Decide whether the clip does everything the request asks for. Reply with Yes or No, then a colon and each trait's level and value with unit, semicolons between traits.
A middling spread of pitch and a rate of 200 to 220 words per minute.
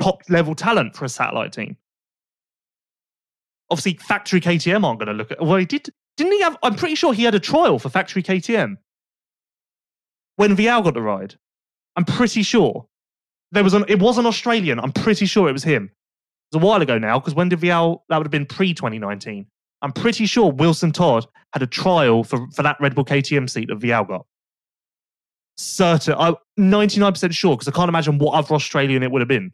No: wide, 7.2 semitones; fast, 205 wpm